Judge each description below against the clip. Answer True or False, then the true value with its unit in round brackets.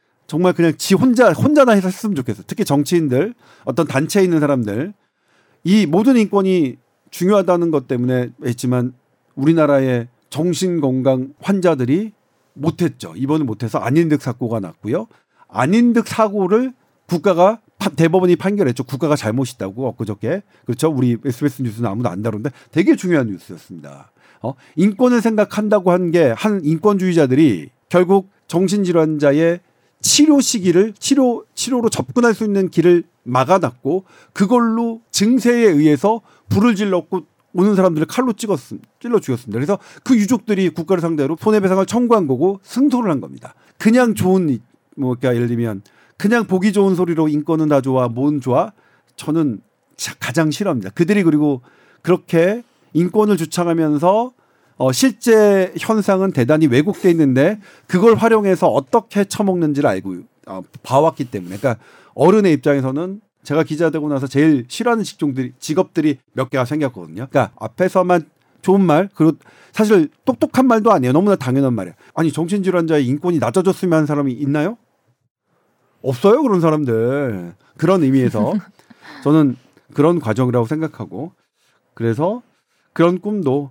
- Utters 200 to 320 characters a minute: False (345 characters per minute)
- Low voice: False (170 Hz)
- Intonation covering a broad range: True (6.7 semitones)